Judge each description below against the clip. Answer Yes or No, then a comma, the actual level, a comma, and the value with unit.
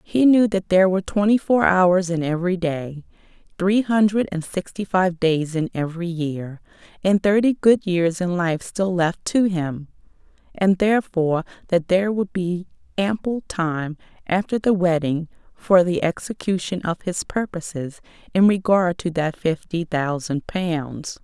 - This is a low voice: No, medium, 180 Hz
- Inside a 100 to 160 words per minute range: Yes, average, 155 wpm